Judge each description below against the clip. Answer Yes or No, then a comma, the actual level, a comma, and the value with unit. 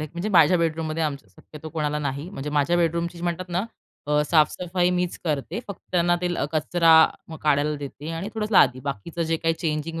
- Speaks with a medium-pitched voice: Yes, medium, 165 Hz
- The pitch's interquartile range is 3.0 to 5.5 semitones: No, narrow, 2.5 semitones